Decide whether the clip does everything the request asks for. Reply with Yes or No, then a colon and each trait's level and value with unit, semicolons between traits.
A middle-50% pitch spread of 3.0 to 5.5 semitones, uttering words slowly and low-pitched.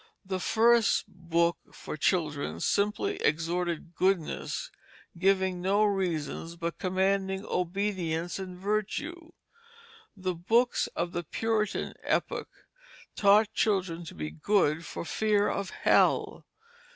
No: average, 3.3 semitones; slow, 110 wpm; medium, 185 Hz